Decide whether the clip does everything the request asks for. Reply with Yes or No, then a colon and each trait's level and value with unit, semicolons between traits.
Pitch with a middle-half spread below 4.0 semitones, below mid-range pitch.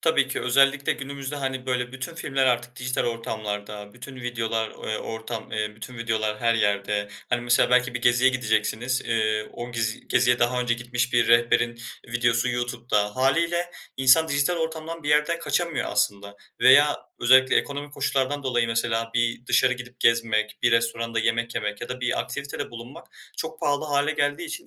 Yes: average, 2.8 semitones; low, 120 Hz